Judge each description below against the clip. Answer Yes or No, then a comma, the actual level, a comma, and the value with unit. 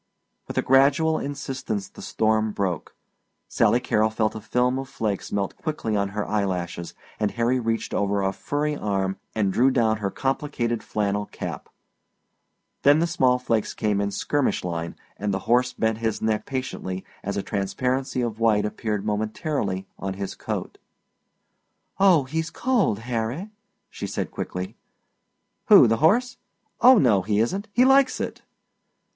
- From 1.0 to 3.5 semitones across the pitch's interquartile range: No, average, 4.9 semitones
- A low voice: Yes, low, 110 Hz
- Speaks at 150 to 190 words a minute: Yes, average, 155 wpm